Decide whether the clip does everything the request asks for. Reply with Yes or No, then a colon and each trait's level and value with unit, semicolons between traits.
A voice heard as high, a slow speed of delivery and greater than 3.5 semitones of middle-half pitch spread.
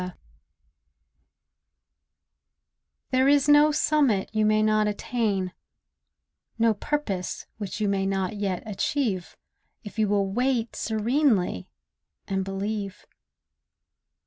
Yes: high, 215 Hz; slow, 100 wpm; average, 4.1 semitones